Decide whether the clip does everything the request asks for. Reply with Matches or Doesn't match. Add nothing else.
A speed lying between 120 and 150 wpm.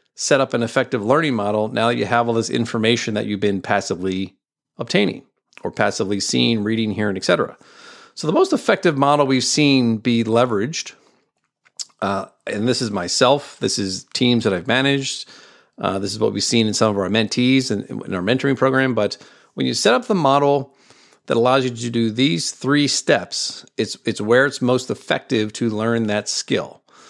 Doesn't match